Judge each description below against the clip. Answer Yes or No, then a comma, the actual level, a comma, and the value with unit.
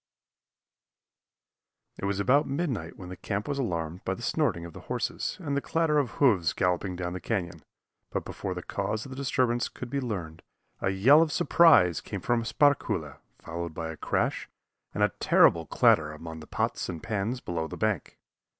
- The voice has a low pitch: Yes, low, 100 Hz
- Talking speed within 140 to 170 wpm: No, average, 185 wpm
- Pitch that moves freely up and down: Yes, wide, 7.9 semitones